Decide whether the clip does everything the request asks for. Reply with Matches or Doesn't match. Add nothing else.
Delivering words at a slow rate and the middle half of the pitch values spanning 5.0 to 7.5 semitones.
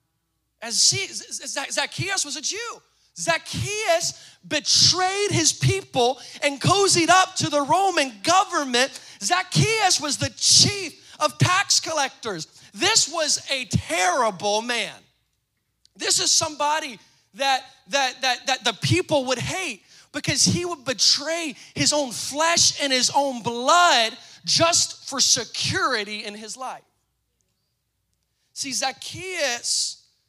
Matches